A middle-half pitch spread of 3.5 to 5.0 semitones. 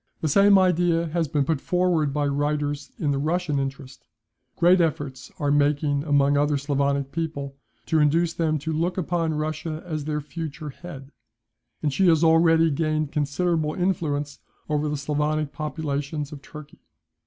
No: narrow, 2.4 semitones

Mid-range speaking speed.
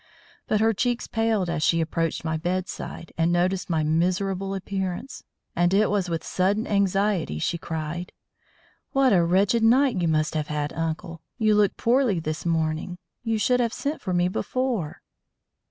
Yes: average, 165 wpm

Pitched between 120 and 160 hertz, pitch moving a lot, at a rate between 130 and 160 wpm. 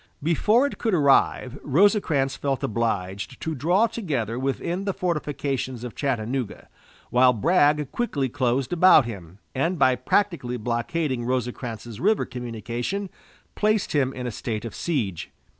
Yes: low, 135 Hz; wide, 6.1 semitones; slow, 135 wpm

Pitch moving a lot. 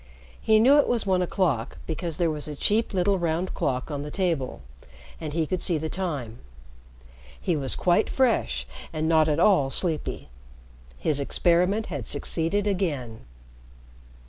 No: average, 4.4 semitones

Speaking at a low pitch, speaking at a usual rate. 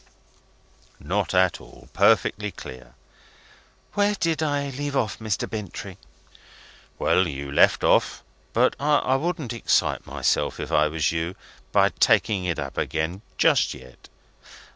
No: low, 105 Hz; slow, 130 wpm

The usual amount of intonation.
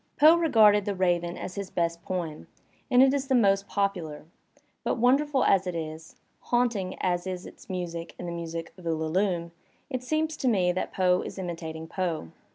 Yes: average, 5.0 semitones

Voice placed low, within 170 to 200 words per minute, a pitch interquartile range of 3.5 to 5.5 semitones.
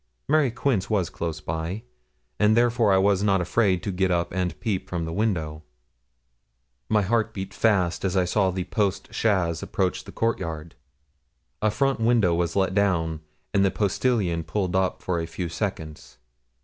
Yes: very low, 95 Hz; average, 175 wpm; average, 3.8 semitones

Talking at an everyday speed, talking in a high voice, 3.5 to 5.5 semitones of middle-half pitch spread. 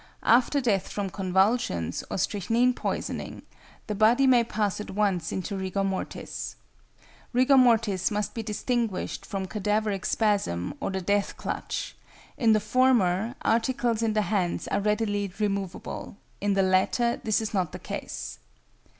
No: average, 145 wpm; high, 210 Hz; average, 3.0 semitones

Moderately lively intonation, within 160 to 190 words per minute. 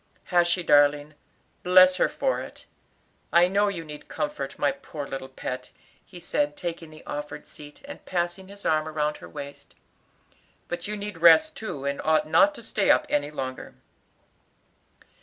Yes: average, 4.2 semitones; average, 165 wpm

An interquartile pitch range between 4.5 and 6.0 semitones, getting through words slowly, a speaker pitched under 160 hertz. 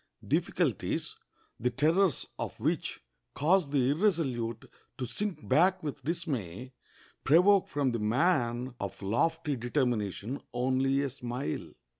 Yes: average, 5.1 semitones; slow, 115 wpm; low, 135 Hz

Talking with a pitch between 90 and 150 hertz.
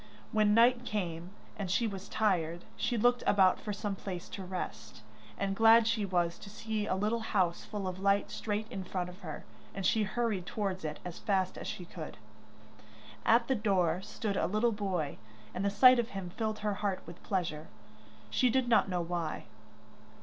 No: high, 200 Hz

